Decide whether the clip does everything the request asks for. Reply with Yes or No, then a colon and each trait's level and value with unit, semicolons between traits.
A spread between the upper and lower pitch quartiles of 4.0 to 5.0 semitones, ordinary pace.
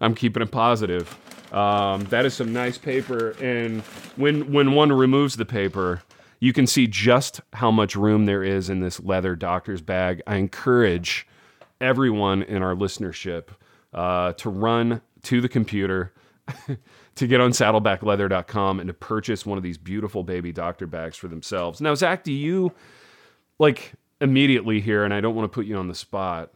Yes: average, 4.5 semitones; average, 170 wpm